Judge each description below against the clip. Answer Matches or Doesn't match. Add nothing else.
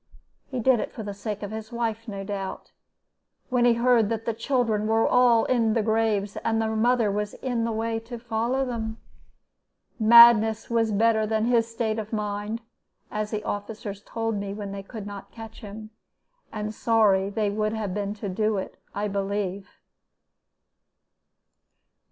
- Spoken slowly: Doesn't match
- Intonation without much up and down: Matches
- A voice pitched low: Doesn't match